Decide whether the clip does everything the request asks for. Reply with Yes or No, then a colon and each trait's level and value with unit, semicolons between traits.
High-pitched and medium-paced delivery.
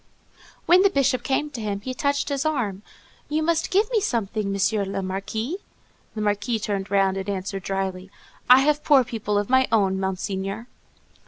Yes: high, 215 Hz; average, 175 wpm